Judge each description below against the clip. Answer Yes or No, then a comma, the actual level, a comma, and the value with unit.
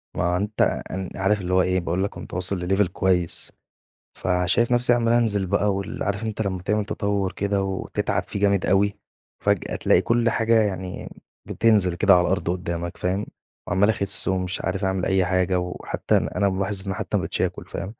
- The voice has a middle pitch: No, very low, 95 Hz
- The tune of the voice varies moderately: No, narrow, 2.0 semitones